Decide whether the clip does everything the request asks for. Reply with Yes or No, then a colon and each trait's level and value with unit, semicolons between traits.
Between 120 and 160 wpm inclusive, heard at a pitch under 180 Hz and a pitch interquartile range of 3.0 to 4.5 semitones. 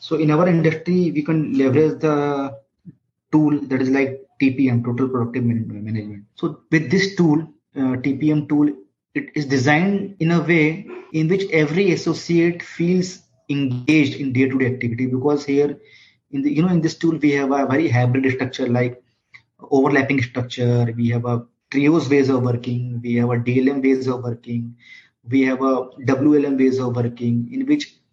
No: average, 170 wpm; low, 135 Hz; average, 3.8 semitones